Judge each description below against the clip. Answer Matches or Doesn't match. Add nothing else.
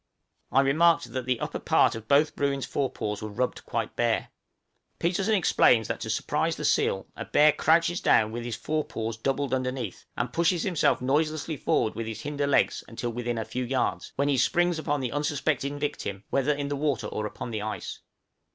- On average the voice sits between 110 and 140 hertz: Matches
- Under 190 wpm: Doesn't match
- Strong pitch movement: Doesn't match